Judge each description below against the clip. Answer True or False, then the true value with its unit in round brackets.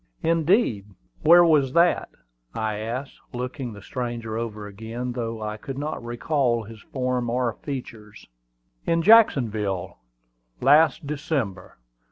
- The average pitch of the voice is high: False (120 Hz)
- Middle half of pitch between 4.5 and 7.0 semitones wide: True (4.8 semitones)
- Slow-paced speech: True (120 wpm)